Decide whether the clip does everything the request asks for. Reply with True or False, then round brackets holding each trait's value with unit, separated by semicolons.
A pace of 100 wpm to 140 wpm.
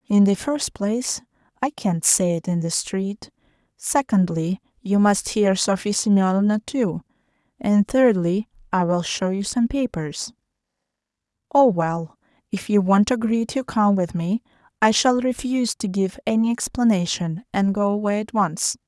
False (155 wpm)